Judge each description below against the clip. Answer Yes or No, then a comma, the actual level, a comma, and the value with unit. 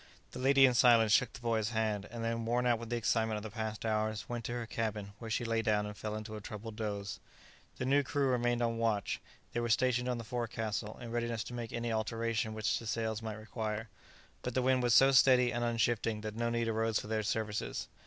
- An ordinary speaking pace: No, fast, 235 wpm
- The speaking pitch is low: Yes, low, 115 Hz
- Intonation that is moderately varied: No, narrow, 1.7 semitones